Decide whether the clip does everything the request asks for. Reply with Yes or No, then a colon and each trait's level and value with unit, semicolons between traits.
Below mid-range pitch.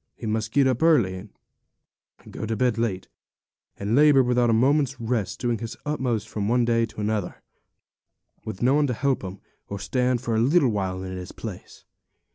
Yes: low, 115 Hz